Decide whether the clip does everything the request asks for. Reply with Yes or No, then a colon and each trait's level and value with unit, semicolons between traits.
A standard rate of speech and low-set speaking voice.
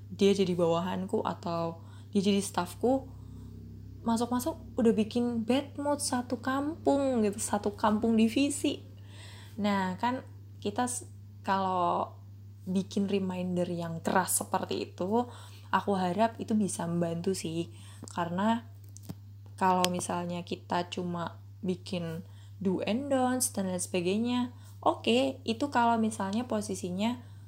No: average, 110 wpm; medium, 185 Hz